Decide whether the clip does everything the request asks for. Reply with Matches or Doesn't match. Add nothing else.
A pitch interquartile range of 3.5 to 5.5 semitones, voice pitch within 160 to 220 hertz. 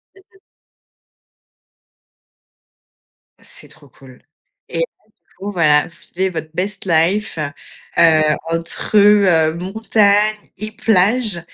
Matches